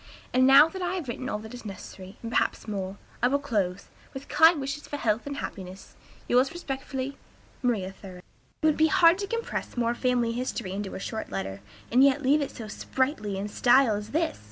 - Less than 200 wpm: No, fast, 205 wpm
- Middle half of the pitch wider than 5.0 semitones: Yes, wide, 5.4 semitones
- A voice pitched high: Yes, high, 245 Hz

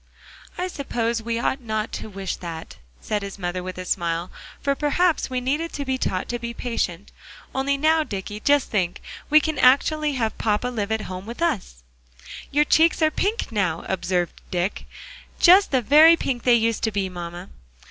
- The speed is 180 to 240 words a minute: Yes, average, 185 wpm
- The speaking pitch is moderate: No, high, 230 Hz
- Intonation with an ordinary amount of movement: No, wide, 7.0 semitones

